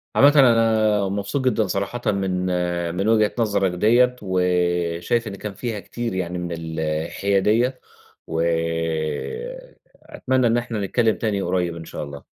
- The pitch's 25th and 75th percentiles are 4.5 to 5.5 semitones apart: Yes, average, 4.8 semitones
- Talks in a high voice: No, low, 100 Hz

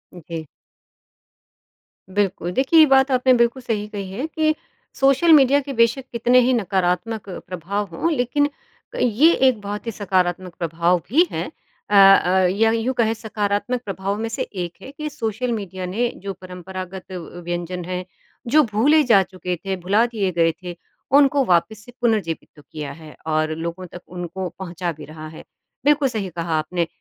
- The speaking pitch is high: Yes, high, 200 Hz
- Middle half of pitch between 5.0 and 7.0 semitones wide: Yes, wide, 5.4 semitones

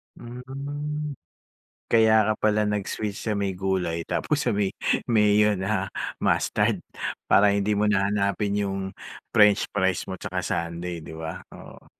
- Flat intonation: Yes, narrow, 2.2 semitones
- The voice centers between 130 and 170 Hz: No, low, 105 Hz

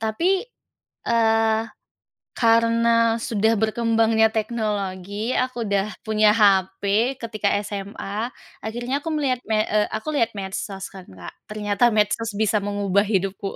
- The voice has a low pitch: No, high, 220 Hz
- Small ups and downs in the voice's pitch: Yes, narrow, 2.2 semitones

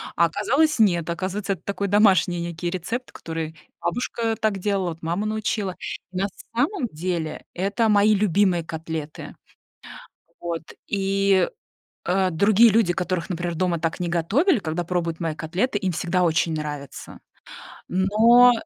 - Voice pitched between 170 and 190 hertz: Yes, medium, 185 Hz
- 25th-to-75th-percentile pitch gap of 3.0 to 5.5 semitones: Yes, average, 3.6 semitones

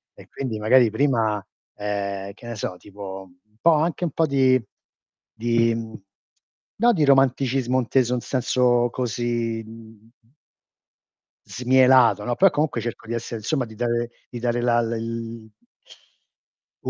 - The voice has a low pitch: Yes, low, 120 Hz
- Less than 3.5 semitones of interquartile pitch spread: Yes, narrow, 2.5 semitones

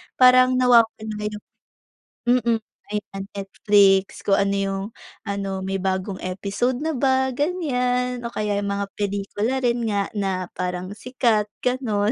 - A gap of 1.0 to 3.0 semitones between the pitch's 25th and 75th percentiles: No, average, 4.1 semitones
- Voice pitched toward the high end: Yes, high, 210 Hz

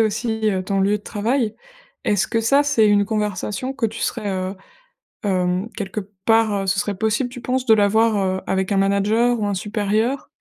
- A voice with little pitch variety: Yes, narrow, 2.3 semitones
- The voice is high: Yes, high, 210 Hz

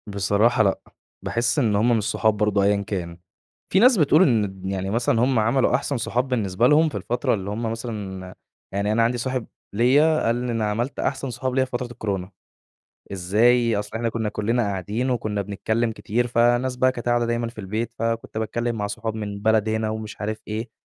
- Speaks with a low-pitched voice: Yes, low, 115 Hz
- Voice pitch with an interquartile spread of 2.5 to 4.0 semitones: Yes, average, 2.8 semitones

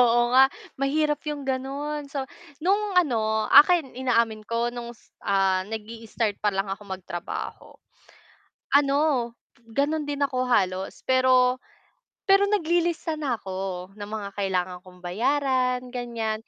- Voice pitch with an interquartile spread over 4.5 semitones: Yes, wide, 5.4 semitones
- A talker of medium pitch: No, high, 245 Hz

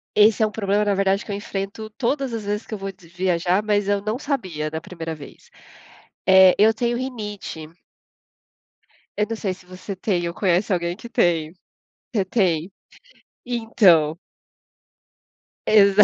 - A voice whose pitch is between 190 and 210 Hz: Yes, high, 200 Hz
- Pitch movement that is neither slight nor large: Yes, average, 3.3 semitones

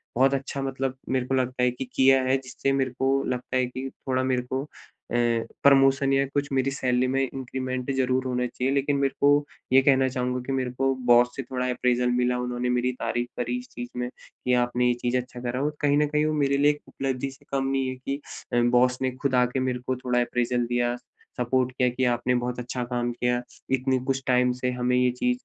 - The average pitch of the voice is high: No, low, 130 Hz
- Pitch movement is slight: Yes, narrow, 1.5 semitones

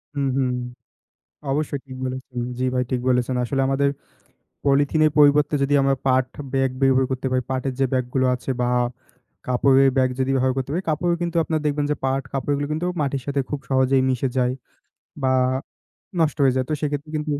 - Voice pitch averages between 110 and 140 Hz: Yes, low, 135 Hz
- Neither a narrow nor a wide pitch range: No, narrow, 1.8 semitones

